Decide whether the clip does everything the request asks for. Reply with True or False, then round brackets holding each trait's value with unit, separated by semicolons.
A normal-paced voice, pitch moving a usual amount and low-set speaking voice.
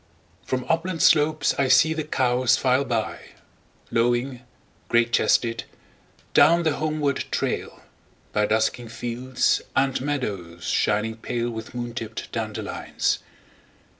False (105 wpm; 3.6 semitones; 125 Hz)